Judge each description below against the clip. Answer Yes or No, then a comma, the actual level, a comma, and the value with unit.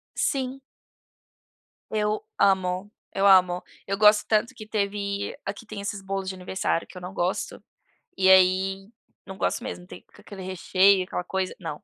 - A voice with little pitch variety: Yes, narrow, 1.8 semitones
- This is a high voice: Yes, high, 195 Hz